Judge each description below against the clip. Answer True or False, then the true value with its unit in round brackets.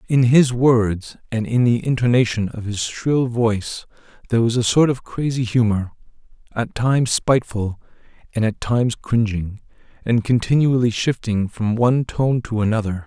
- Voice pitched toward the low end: True (115 Hz)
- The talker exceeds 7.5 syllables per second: False (4.8 syllables/s)